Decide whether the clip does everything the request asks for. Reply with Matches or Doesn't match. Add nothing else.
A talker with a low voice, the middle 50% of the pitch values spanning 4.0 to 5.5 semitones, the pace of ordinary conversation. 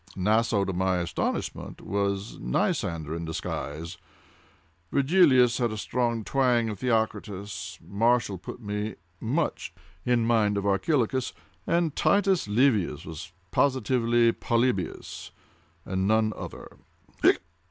Doesn't match